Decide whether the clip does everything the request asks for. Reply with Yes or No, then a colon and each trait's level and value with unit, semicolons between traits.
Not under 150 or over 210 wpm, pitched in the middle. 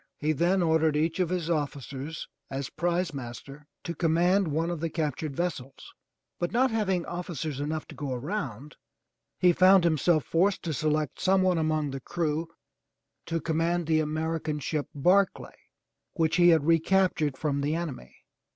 Yes: average, 160 wpm; medium, 160 Hz